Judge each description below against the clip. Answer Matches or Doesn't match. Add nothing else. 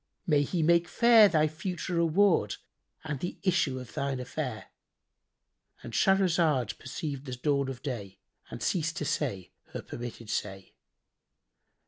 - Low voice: Doesn't match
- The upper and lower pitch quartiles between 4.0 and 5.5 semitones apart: Matches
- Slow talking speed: Matches